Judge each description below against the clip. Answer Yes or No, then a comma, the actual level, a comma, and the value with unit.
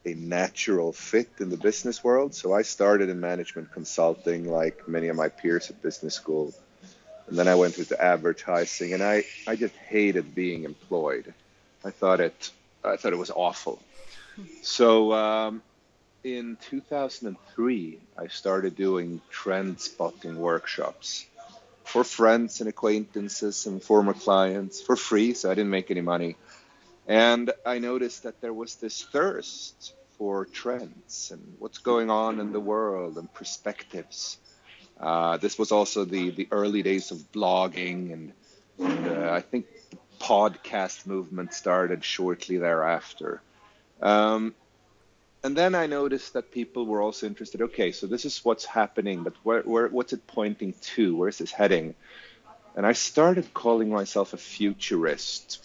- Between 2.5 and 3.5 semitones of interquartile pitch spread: No, average, 4.3 semitones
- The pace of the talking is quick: No, average, 150 wpm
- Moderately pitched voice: No, low, 105 Hz